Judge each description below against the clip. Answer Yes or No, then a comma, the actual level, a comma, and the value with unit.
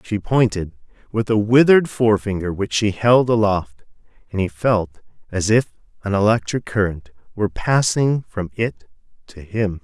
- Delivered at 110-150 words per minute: Yes, average, 145 wpm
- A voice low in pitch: Yes, low, 105 Hz